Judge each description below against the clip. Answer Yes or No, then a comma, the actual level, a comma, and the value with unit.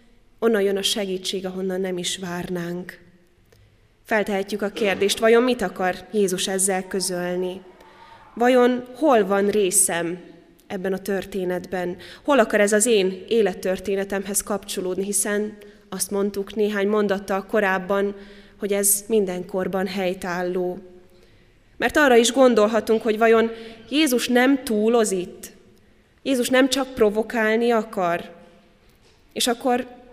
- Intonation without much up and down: No, average, 3.4 semitones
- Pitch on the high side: Yes, high, 200 Hz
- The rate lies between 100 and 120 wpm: Yes, average, 115 wpm